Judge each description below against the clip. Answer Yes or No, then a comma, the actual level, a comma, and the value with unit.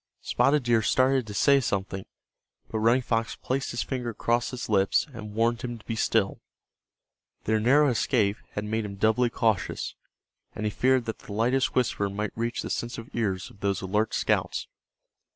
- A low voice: Yes, low, 115 Hz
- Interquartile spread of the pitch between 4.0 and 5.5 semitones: No, average, 2.8 semitones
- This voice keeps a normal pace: Yes, average, 175 wpm